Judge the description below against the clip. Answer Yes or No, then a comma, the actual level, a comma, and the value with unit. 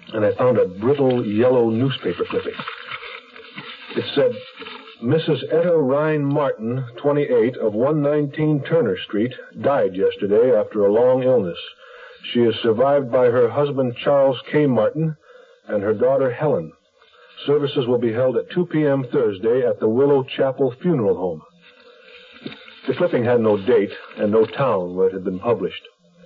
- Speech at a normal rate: Yes, average, 150 wpm